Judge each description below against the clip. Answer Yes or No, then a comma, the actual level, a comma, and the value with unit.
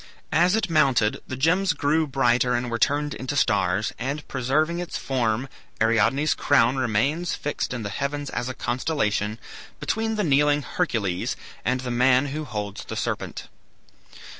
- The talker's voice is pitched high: No, low, 130 Hz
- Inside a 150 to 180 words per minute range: Yes, average, 155 wpm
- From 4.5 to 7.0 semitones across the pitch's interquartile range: No, average, 3.9 semitones